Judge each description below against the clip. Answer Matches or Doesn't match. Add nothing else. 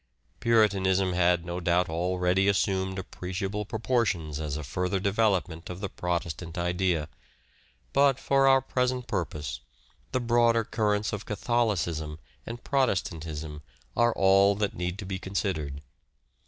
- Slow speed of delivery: Matches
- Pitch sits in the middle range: Doesn't match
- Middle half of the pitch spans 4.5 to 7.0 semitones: Doesn't match